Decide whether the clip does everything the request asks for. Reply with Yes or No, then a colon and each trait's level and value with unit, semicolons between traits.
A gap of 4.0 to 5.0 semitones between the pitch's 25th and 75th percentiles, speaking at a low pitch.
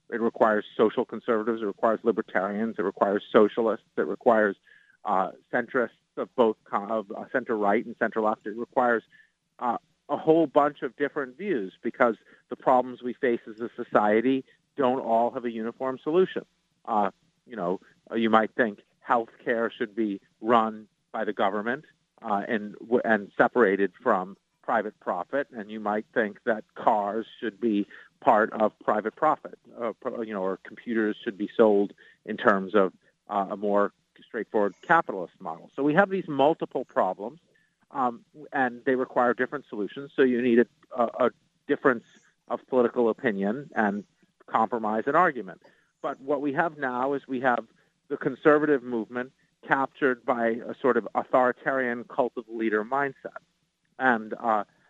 No: average, 3.4 semitones; low, 120 Hz